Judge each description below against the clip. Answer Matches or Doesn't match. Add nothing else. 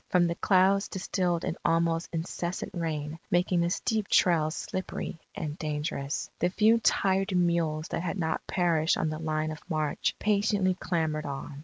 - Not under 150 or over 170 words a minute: Matches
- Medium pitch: Matches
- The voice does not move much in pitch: Doesn't match